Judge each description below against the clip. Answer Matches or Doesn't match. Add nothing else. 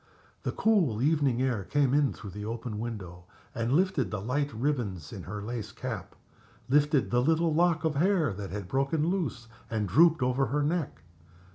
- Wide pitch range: Matches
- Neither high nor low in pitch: Doesn't match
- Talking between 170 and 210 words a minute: Matches